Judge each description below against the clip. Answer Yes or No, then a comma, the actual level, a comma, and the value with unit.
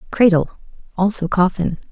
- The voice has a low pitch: No, medium, 185 Hz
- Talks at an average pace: No, slow, 95 wpm